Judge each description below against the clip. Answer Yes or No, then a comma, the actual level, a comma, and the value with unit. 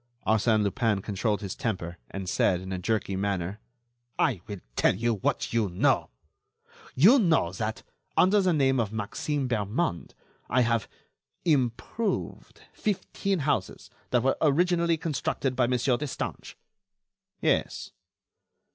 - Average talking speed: No, slow, 130 wpm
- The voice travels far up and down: Yes, wide, 6.5 semitones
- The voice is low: Yes, low, 115 Hz